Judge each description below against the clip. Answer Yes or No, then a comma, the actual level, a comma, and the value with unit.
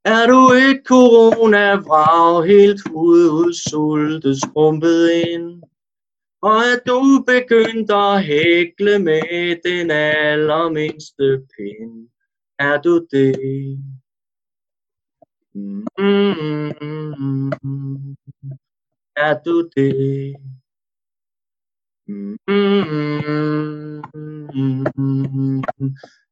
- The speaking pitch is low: No, medium, 155 Hz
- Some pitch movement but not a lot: No, wide, 6.5 semitones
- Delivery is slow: Yes, slow, 60 wpm